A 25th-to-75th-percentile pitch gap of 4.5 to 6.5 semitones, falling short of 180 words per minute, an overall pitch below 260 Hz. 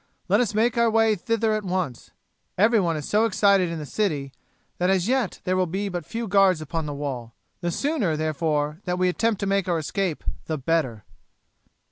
No: average, 5.2 semitones; average, 195 wpm; medium, 185 Hz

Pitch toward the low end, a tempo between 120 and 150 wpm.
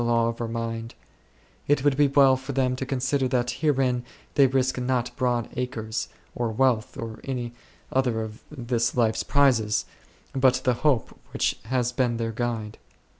No: low, 125 Hz; average, 165 wpm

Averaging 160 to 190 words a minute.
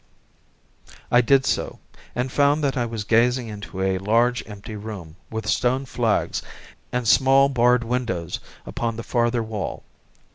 No: average, 145 wpm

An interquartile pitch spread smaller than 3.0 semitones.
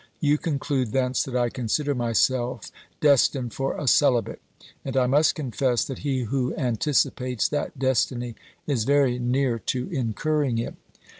Yes: narrow, 2.5 semitones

